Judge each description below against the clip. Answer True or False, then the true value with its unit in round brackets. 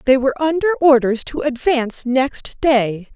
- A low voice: False (265 Hz)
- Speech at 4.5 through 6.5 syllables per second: True (4.6 syllables/s)